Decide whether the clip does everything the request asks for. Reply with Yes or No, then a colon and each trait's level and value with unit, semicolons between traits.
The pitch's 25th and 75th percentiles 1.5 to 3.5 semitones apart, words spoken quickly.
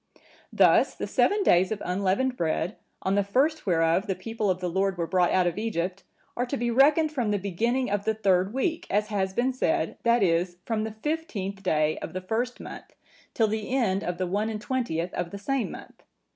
No: average, 4.7 semitones; fast, 215 wpm